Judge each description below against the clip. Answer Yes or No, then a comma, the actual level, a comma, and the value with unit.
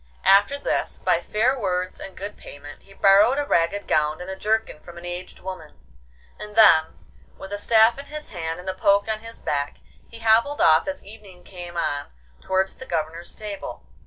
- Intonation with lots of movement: No, average, 4.2 semitones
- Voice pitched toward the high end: Yes, high, 195 Hz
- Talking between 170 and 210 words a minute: Yes, average, 190 wpm